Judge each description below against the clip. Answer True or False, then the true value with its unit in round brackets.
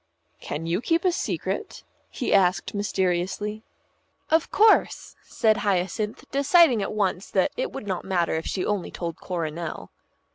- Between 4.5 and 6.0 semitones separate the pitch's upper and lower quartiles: True (5.3 semitones)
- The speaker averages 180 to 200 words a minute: False (145 wpm)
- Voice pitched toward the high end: True (200 Hz)